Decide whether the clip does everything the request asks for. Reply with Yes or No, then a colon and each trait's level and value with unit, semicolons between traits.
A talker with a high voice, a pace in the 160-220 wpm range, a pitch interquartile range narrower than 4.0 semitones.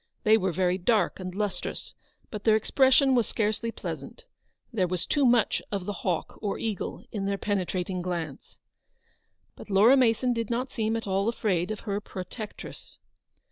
Yes: high, 210 Hz; average, 165 wpm; average, 3.5 semitones